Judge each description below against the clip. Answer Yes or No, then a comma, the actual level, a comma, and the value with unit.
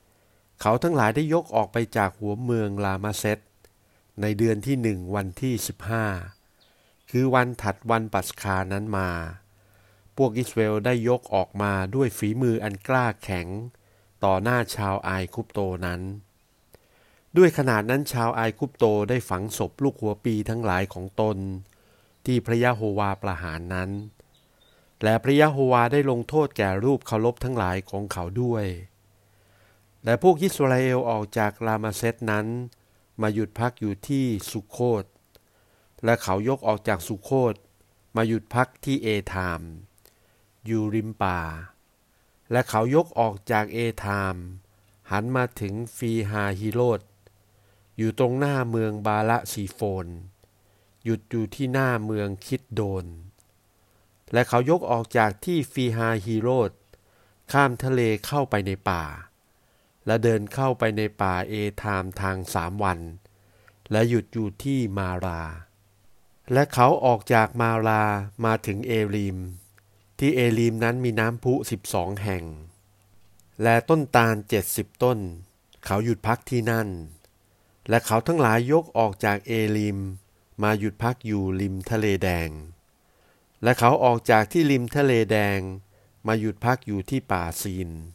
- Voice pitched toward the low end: Yes, low, 105 Hz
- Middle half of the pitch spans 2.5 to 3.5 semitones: Yes, average, 3.2 semitones